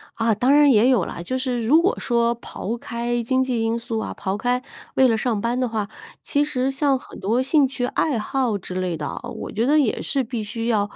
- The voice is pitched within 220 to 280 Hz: Yes, high, 240 Hz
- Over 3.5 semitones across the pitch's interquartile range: No, average, 2.9 semitones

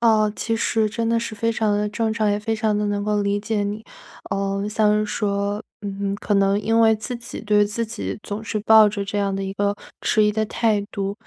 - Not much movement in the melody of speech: Yes, narrow, 1.4 semitones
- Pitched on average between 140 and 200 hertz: No, high, 210 Hz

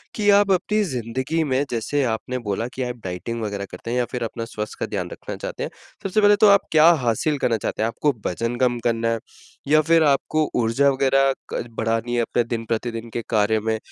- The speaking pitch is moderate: No, low, 120 Hz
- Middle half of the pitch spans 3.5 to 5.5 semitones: Yes, average, 4.2 semitones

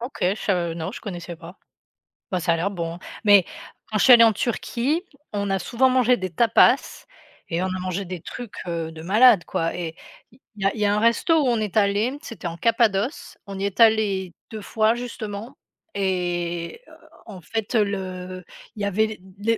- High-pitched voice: Yes, high, 200 Hz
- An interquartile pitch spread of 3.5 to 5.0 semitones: Yes, average, 4.1 semitones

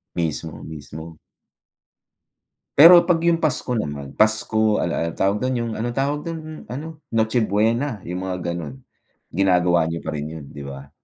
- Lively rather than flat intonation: Yes, wide, 8.3 semitones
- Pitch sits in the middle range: No, low, 100 Hz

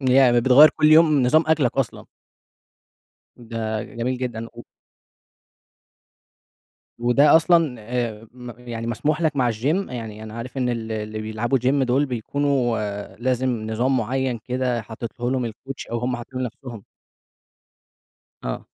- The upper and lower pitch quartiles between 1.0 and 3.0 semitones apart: Yes, narrow, 2.5 semitones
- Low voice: Yes, low, 125 Hz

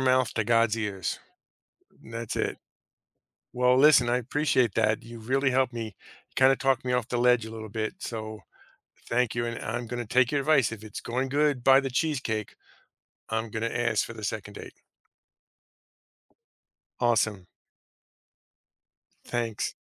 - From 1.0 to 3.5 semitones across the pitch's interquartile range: Yes, narrow, 2.6 semitones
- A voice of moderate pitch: No, low, 120 Hz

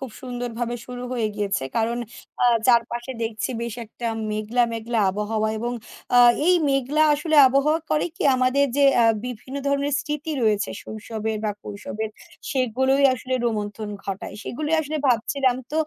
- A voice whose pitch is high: Yes, high, 240 Hz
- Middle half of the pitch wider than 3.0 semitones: Yes, average, 3.8 semitones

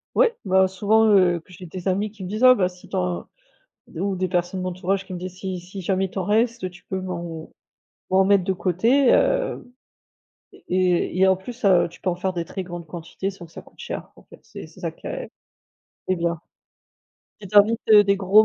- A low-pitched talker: No, medium, 185 Hz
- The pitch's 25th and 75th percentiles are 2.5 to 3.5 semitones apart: No, narrow, 2.0 semitones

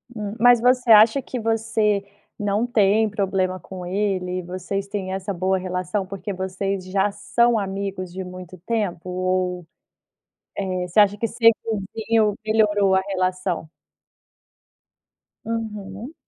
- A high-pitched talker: Yes, high, 195 Hz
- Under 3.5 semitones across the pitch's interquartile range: Yes, average, 2.7 semitones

